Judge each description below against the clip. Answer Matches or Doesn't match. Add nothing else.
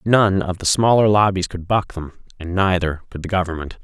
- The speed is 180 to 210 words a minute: Matches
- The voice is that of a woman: Doesn't match